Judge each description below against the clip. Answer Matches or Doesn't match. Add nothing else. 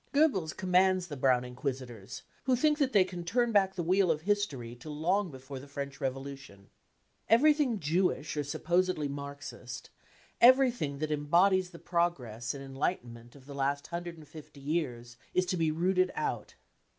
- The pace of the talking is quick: Doesn't match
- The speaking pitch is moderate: Matches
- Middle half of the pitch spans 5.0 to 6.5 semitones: Matches